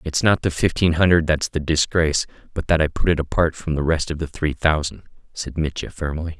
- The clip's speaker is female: No, male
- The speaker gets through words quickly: Yes, fast, 225 wpm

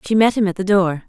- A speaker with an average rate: No, fast, 335 wpm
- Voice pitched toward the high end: Yes, high, 195 Hz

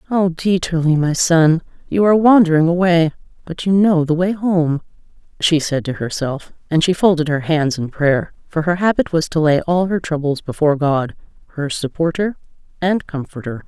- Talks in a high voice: No, medium, 165 Hz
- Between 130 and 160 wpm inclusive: No, average, 175 wpm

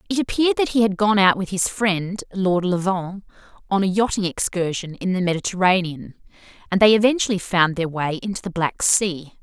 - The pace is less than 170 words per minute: No, average, 185 wpm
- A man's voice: No, female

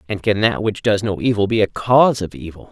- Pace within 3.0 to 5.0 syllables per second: No, 5.9 syllables/s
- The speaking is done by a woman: No, male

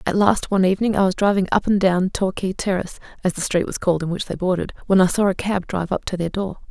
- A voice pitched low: No, high, 190 Hz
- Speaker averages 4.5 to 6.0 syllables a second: No, 6.8 syllables/s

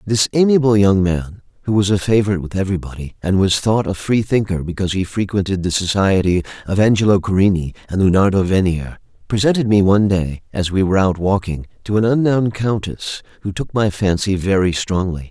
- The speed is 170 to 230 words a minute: Yes, average, 180 wpm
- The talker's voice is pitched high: No, low, 100 Hz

